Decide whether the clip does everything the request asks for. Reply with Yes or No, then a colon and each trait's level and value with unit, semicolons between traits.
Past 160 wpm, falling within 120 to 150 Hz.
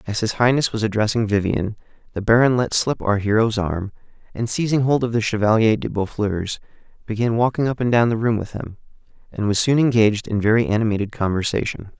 No: average, 190 wpm; low, 110 Hz